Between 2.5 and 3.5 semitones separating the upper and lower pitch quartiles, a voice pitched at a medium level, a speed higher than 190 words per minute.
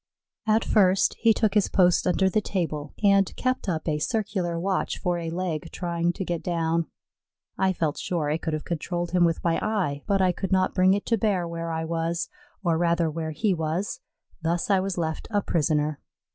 Yes: average, 2.9 semitones; medium, 175 Hz; average, 200 wpm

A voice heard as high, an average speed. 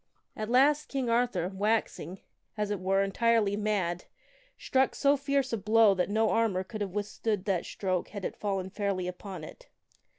Yes: high, 205 Hz; average, 170 wpm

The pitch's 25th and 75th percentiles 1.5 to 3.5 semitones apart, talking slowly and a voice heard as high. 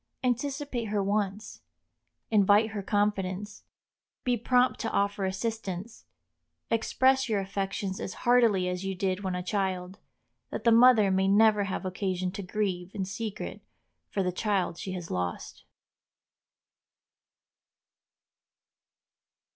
Yes: average, 2.8 semitones; slow, 120 wpm; high, 200 Hz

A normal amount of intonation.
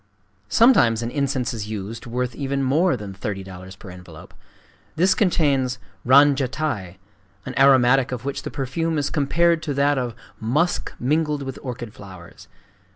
Yes: average, 4.4 semitones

